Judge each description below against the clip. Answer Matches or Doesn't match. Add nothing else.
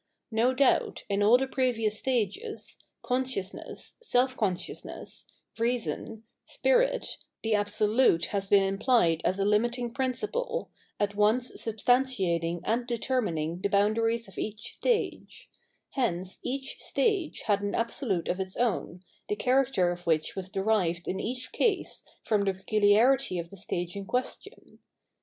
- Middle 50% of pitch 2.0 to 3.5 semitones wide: Doesn't match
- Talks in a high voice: Matches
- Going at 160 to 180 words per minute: Doesn't match